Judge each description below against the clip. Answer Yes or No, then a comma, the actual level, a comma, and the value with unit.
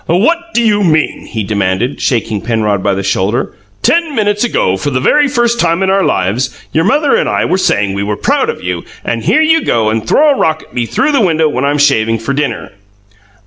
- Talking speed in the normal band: No, fast, 225 wpm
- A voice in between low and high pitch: Yes, medium, 150 Hz